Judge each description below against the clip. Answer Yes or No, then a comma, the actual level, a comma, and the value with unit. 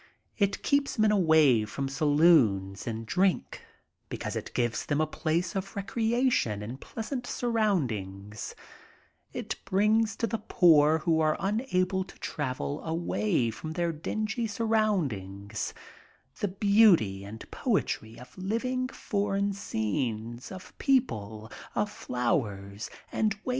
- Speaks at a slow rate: Yes, slow, 130 wpm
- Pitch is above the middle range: No, medium, 165 Hz